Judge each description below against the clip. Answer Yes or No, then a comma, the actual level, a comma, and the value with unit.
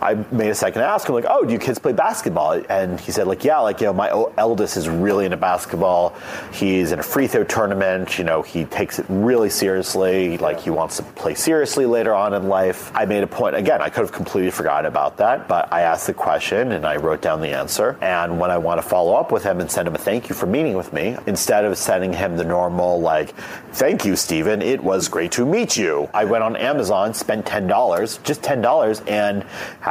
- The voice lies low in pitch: Yes, very low, 95 Hz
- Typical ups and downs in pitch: No, narrow, 1.8 semitones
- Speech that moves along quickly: Yes, fast, 240 wpm